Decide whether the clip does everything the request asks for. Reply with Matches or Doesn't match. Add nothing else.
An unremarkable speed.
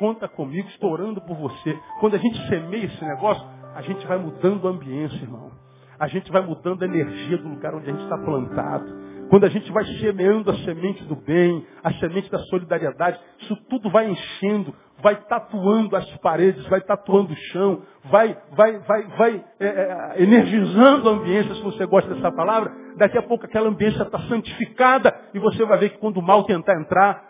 Doesn't match